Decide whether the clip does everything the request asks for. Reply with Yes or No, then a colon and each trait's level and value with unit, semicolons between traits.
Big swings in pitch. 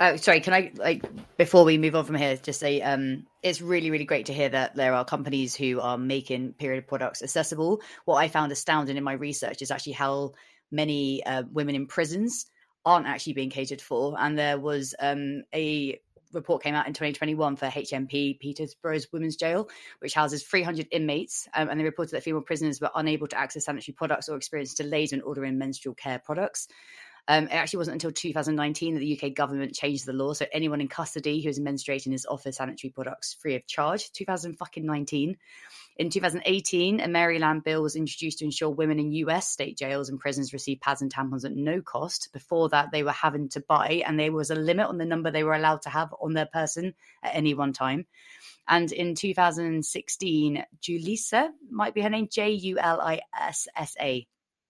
No: average, 2.8 semitones